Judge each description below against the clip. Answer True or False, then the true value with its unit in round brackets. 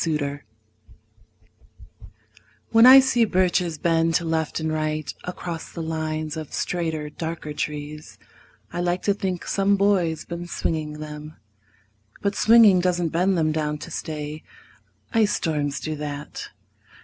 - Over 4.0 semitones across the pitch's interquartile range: False (2.8 semitones)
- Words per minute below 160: True (135 wpm)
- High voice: False (160 Hz)